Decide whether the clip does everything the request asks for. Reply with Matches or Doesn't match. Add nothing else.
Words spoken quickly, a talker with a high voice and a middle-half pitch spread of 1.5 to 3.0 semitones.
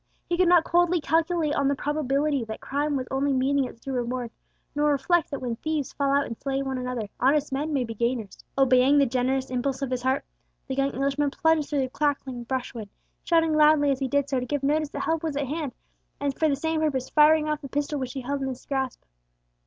Matches